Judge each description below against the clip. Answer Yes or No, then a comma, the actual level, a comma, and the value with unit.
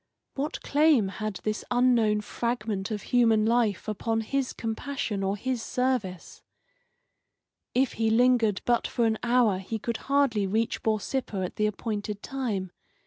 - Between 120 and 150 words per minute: Yes, average, 140 wpm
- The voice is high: Yes, high, 225 Hz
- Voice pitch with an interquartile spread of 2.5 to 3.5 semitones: Yes, average, 2.9 semitones